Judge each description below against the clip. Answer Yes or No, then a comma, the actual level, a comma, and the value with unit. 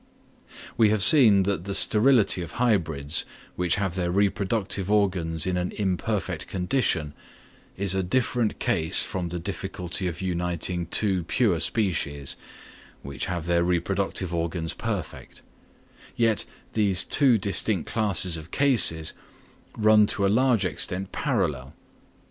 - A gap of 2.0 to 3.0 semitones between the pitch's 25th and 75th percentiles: No, average, 3.6 semitones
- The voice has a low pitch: Yes, very low, 95 Hz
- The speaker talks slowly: Yes, slow, 130 wpm